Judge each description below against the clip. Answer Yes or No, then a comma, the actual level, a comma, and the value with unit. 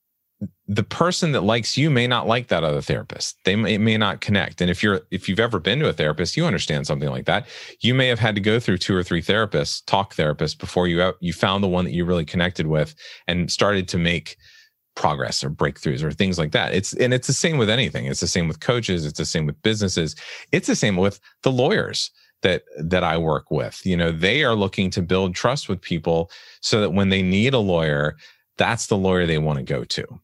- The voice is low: Yes, very low, 95 Hz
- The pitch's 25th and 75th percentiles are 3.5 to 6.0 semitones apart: Yes, average, 4.3 semitones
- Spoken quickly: Yes, fast, 235 wpm